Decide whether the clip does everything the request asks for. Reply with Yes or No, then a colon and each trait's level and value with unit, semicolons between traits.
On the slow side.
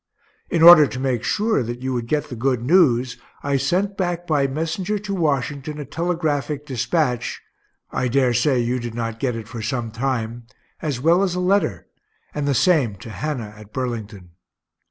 No: average, 180 wpm